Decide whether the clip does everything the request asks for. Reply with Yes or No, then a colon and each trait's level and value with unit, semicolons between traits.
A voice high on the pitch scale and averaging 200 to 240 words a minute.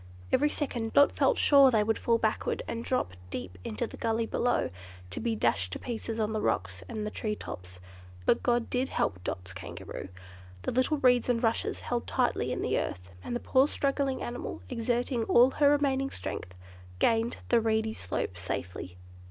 No: high, 230 Hz; average, 185 wpm